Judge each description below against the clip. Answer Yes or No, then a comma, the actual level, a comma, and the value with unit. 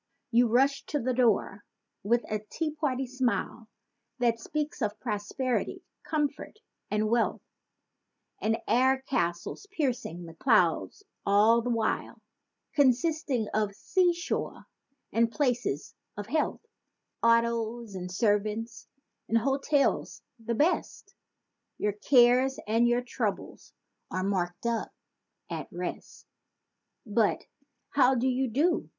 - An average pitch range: Yes, average, 3.8 semitones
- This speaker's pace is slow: Yes, slow, 110 wpm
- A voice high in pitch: Yes, high, 235 Hz